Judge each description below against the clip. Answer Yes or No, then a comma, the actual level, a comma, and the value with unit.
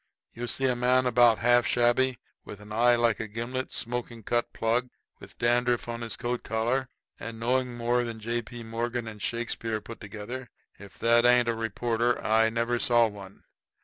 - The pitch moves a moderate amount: No, narrow, 1.4 semitones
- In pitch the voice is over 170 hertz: No, low, 120 Hz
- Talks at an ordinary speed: Yes, average, 180 wpm